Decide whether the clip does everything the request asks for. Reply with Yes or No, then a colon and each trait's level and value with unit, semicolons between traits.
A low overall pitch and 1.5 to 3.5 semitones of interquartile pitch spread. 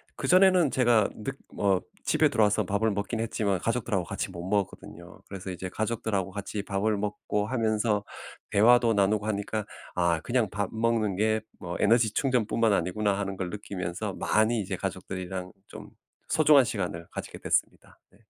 Yes: low, 105 Hz; average, 2.7 semitones